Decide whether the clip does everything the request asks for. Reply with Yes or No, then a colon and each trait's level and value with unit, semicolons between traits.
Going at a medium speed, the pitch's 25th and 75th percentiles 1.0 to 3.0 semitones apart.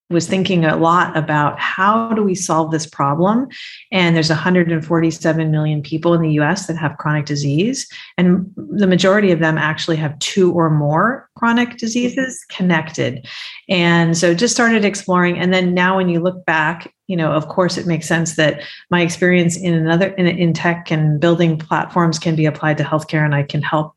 Yes: average, 185 wpm; average, 2.7 semitones